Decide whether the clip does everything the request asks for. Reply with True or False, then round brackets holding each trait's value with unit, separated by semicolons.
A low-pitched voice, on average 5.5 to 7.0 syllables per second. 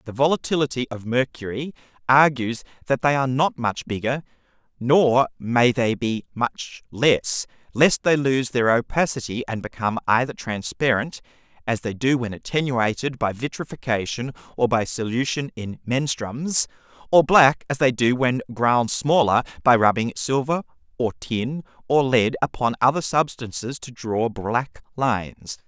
False (125 Hz; 4.5 syllables/s)